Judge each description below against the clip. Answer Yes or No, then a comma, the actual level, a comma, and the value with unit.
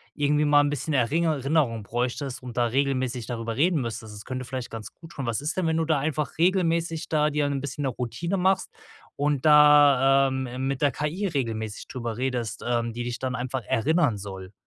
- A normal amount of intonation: Yes, average, 3.9 semitones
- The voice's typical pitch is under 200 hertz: Yes, low, 135 Hz